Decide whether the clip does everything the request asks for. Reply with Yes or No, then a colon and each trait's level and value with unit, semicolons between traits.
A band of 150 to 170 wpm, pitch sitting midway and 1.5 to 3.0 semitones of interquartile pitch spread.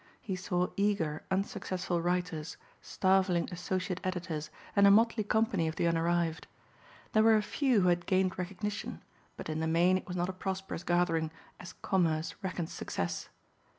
Yes: average, 160 wpm; medium, 180 Hz; narrow, 2.4 semitones